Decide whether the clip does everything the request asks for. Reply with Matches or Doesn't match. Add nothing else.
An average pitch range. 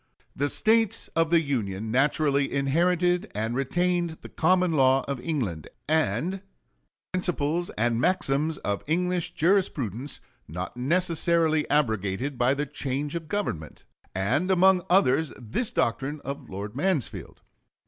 Doesn't match